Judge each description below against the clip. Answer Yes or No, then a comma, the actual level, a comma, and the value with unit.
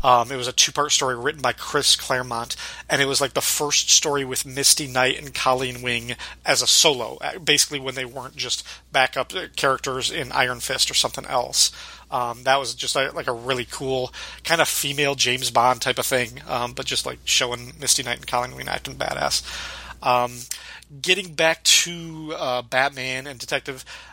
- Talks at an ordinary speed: Yes, average, 185 wpm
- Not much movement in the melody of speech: Yes, narrow, 2.1 semitones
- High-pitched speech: No, low, 130 Hz